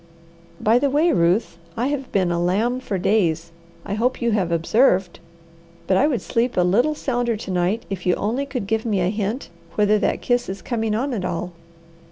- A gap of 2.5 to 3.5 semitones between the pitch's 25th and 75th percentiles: No, average, 5.0 semitones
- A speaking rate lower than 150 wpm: No, fast, 205 wpm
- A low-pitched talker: No, high, 215 Hz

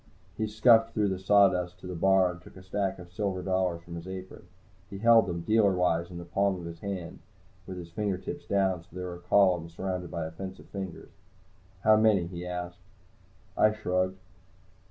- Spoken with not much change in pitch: Yes, narrow, 2.1 semitones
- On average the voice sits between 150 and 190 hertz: No, very low, 95 Hz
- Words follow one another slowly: No, average, 200 wpm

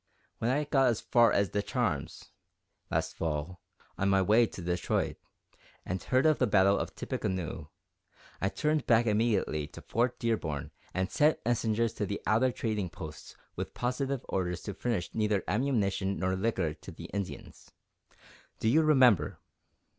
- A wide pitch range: No, average, 4.3 semitones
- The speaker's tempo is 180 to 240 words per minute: No, average, 155 wpm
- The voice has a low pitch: Yes, low, 105 Hz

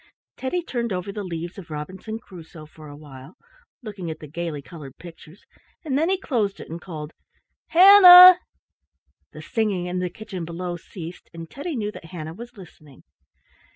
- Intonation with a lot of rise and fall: Yes, wide, 5.7 semitones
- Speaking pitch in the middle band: Yes, medium, 180 Hz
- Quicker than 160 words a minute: Yes, average, 170 wpm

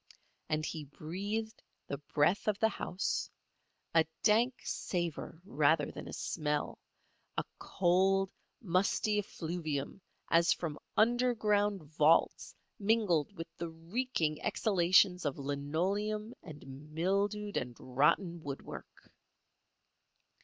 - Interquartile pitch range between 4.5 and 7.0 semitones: Yes, average, 5.2 semitones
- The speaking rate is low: Yes, slow, 95 wpm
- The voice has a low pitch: No, medium, 175 Hz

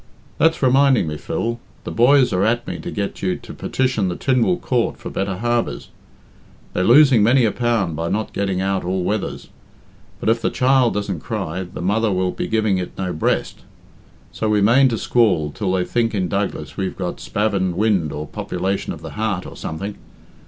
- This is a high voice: No, low, 105 Hz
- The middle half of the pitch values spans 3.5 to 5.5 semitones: Yes, average, 4.3 semitones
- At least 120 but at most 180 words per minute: No, average, 195 wpm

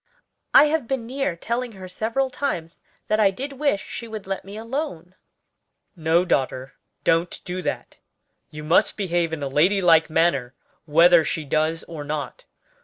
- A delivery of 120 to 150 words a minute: No, average, 165 wpm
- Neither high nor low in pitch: Yes, medium, 180 Hz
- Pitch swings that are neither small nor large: No, wide, 6.0 semitones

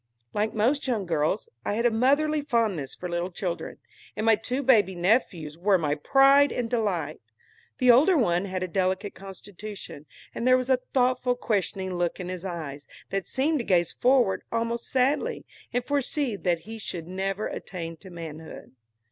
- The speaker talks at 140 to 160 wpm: No, average, 175 wpm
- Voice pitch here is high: Yes, high, 205 Hz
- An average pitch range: No, wide, 6.0 semitones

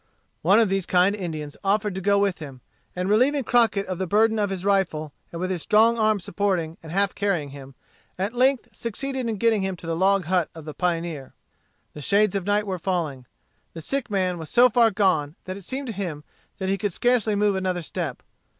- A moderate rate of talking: No, fast, 215 wpm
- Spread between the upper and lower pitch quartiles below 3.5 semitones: No, average, 3.8 semitones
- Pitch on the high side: Yes, high, 195 Hz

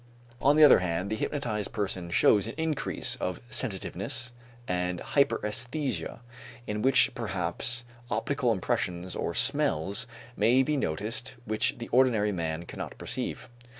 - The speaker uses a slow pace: Yes, slow, 130 wpm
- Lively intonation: Yes, wide, 6.0 semitones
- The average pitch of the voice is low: Yes, low, 110 Hz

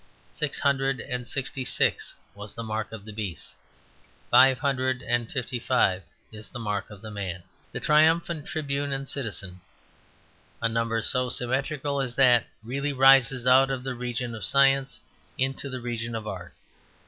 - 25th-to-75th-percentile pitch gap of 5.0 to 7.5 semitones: No, average, 3.3 semitones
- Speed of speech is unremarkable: Yes, average, 160 wpm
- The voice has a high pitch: No, low, 125 Hz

